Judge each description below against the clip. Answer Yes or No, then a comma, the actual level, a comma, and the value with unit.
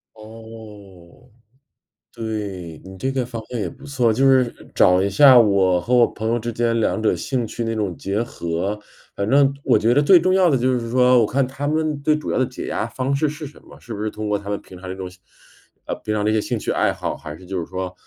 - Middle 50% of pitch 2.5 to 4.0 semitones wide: No, average, 4.5 semitones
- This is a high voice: No, low, 115 Hz